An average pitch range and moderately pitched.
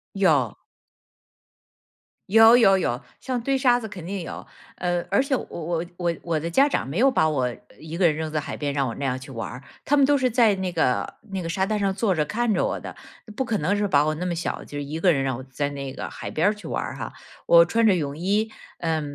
No: wide, 6.0 semitones; medium, 175 Hz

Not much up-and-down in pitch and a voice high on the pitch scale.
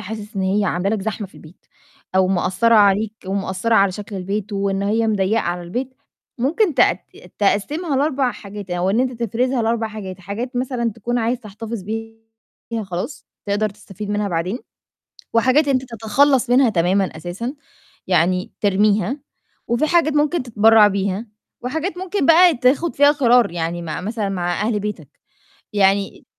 No: average, 4.2 semitones; high, 215 Hz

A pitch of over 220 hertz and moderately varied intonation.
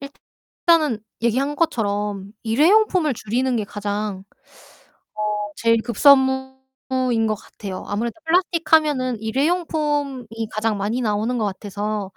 Yes: high, 240 Hz; average, 5.0 semitones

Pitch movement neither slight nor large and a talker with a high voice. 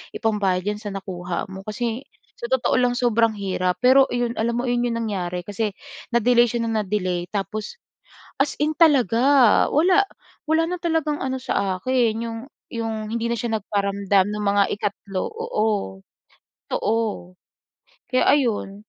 Yes: average, 3.9 semitones; high, 225 Hz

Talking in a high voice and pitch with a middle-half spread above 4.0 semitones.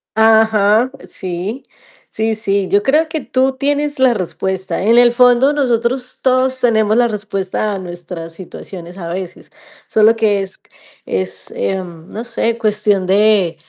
Yes: high, 215 Hz; average, 4.4 semitones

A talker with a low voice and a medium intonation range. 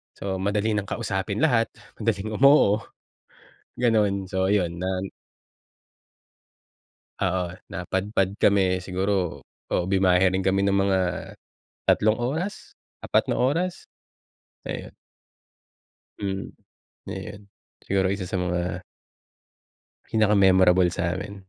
No: very low, 95 Hz; narrow, 2.0 semitones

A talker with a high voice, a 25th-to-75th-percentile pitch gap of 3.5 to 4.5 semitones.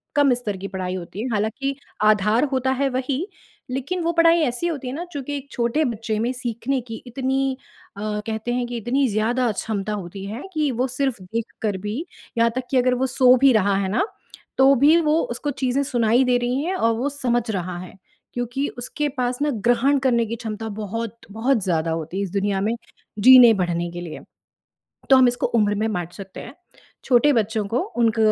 Yes: high, 240 Hz; average, 3.9 semitones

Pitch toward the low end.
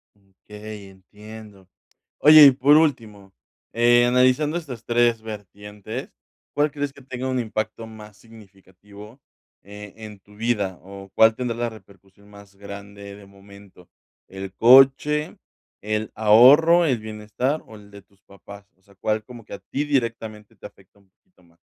Yes: low, 110 Hz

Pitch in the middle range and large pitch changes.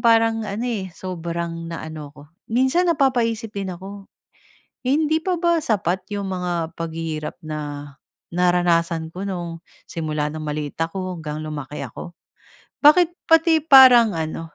Yes: medium, 180 Hz; wide, 6.3 semitones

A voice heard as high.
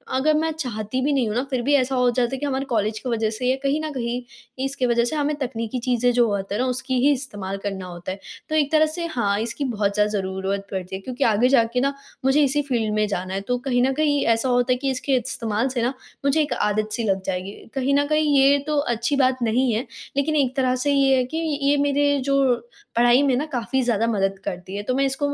Yes: very high, 250 Hz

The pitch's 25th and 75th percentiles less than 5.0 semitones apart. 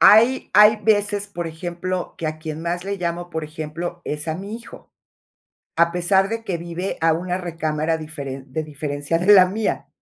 Yes: average, 3.5 semitones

